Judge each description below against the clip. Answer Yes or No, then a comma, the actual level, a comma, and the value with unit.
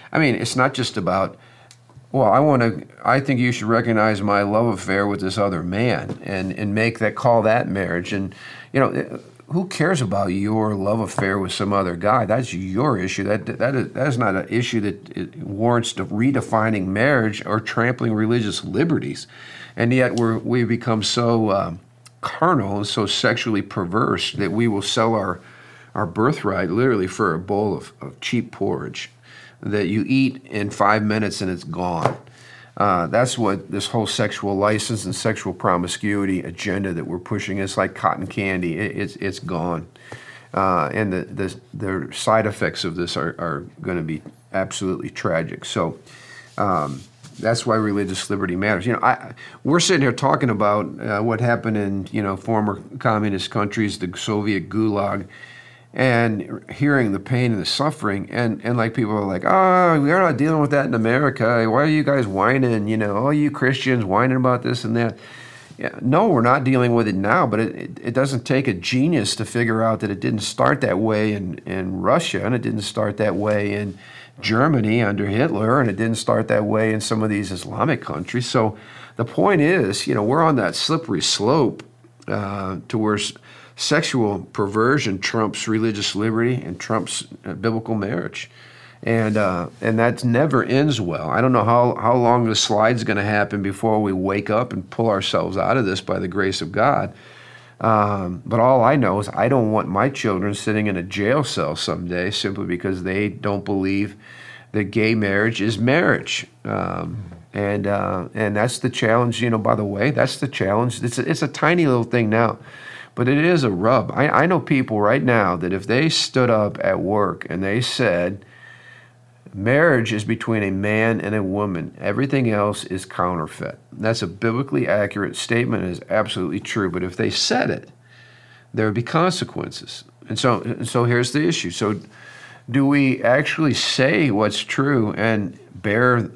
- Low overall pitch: Yes, low, 110 Hz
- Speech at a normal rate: Yes, average, 185 wpm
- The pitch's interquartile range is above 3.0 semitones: Yes, average, 3.5 semitones